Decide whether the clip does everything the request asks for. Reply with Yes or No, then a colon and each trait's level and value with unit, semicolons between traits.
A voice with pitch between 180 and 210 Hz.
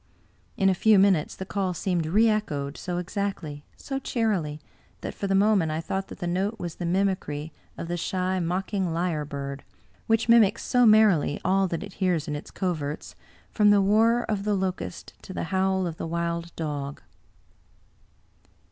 Yes: medium, 185 Hz